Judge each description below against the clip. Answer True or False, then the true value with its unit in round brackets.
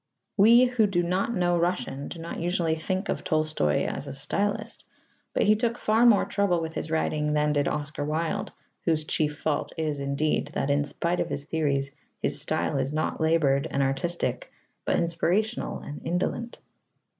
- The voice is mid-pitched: True (160 Hz)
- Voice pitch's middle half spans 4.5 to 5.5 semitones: False (4.0 semitones)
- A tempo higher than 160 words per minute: True (175 wpm)